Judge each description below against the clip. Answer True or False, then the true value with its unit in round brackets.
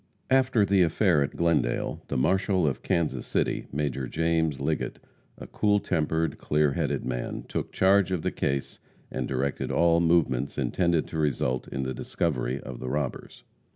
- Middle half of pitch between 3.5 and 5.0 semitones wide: True (4.2 semitones)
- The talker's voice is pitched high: False (80 Hz)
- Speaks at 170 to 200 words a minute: False (160 wpm)